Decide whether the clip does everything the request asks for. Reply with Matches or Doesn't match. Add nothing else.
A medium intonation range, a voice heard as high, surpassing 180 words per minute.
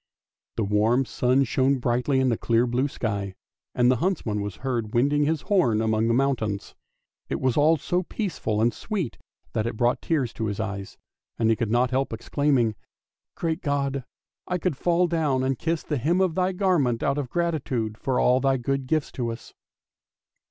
Doesn't match